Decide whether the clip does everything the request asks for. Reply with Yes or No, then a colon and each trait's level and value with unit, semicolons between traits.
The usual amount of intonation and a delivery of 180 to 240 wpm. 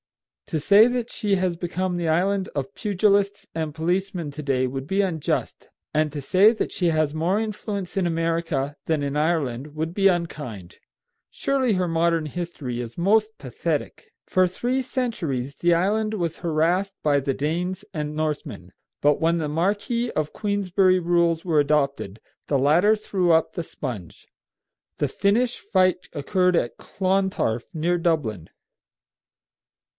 No: average, 4.5 semitones; average, 150 wpm